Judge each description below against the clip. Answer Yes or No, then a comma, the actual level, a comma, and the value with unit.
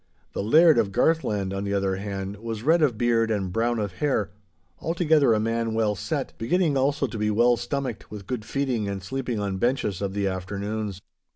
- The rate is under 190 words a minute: No, average, 195 wpm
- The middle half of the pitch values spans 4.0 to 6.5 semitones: Yes, average, 4.5 semitones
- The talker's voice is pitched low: Yes, low, 110 Hz